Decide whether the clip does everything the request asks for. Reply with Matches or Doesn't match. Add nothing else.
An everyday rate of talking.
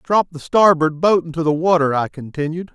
Matches